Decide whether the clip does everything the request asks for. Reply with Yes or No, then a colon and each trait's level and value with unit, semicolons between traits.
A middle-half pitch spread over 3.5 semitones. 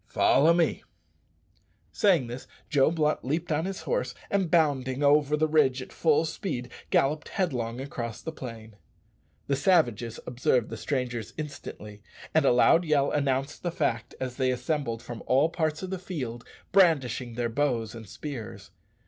Yes: average, 4.5 semitones